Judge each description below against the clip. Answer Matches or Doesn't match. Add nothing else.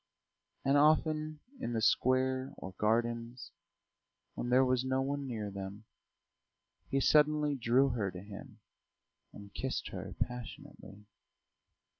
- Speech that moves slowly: Matches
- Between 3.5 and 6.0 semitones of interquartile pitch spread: Matches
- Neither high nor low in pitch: Doesn't match